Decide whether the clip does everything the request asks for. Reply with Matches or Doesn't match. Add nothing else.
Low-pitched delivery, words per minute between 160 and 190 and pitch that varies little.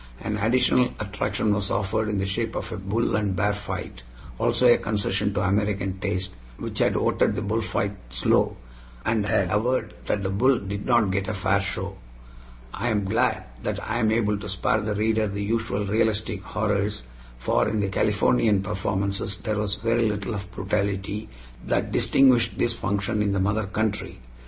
Matches